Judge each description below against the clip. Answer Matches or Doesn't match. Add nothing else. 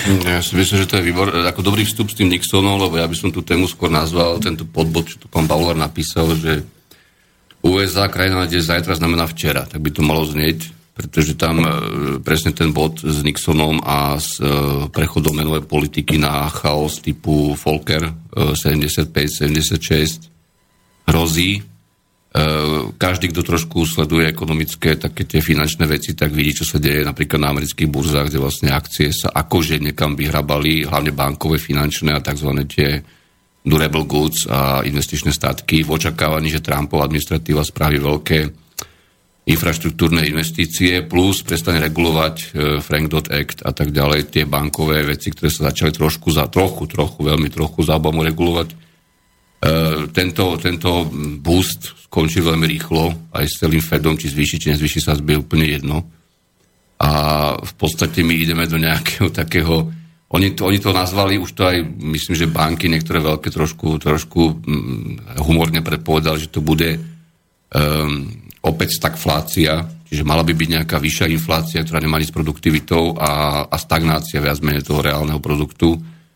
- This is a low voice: Matches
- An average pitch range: Doesn't match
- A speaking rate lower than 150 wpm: Doesn't match